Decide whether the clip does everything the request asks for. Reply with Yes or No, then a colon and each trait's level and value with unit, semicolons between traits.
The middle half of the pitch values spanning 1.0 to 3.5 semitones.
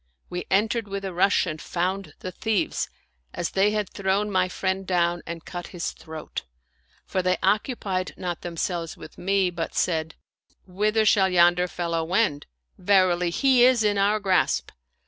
Yes: narrow, 2.6 semitones